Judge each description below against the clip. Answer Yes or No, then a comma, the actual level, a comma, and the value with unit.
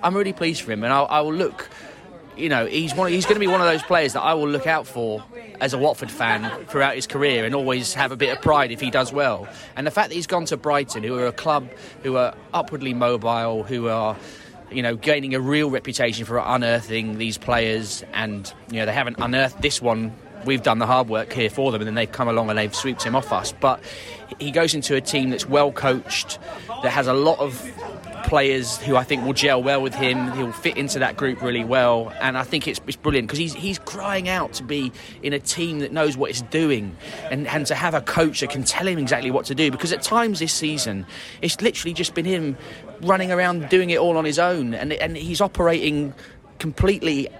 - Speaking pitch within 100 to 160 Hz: Yes, medium, 140 Hz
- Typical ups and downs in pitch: Yes, average, 4.8 semitones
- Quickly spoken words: Yes, fast, 240 wpm